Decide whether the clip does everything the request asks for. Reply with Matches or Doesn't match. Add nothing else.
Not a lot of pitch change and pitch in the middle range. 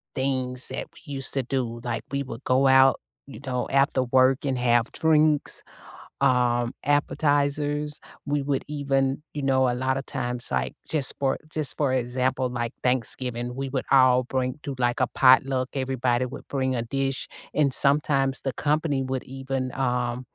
Doesn't match